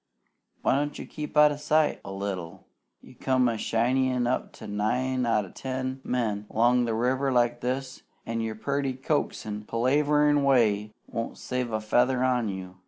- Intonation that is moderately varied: Yes, average, 3.3 semitones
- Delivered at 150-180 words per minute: Yes, average, 170 wpm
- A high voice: No, low, 125 Hz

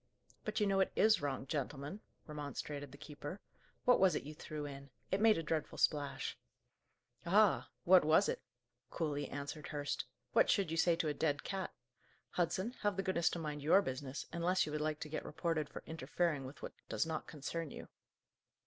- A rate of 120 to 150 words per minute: No, average, 190 wpm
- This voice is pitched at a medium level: Yes, medium, 155 Hz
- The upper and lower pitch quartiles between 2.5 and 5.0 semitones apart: Yes, average, 4.2 semitones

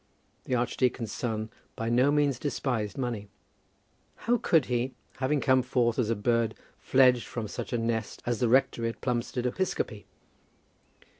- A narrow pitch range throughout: Yes, narrow, 2.2 semitones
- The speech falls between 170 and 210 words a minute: No, average, 150 wpm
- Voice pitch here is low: Yes, low, 120 Hz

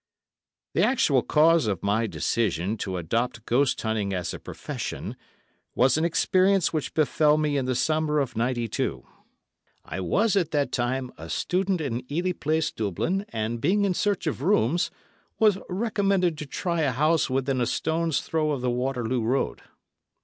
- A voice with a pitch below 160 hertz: Yes, medium, 140 Hz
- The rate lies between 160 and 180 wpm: Yes, average, 165 wpm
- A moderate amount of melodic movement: No, wide, 6.1 semitones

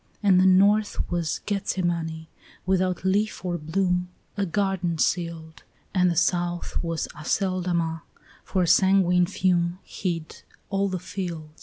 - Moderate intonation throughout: No, narrow, 2.0 semitones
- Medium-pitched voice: Yes, medium, 180 Hz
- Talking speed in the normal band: No, slow, 130 wpm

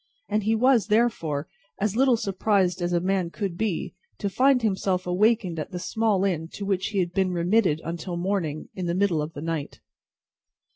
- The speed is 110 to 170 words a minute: No, average, 190 wpm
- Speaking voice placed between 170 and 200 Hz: Yes, high, 190 Hz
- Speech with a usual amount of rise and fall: Yes, average, 3.6 semitones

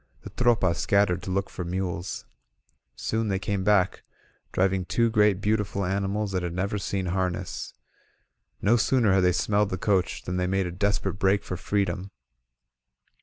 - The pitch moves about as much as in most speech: No, narrow, 2.0 semitones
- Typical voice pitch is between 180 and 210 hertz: No, very low, 95 Hz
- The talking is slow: No, average, 165 wpm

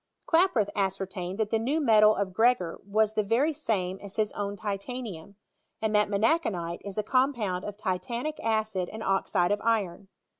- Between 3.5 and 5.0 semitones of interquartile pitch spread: No, average, 2.9 semitones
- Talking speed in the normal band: Yes, average, 165 wpm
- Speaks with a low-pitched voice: No, high, 210 Hz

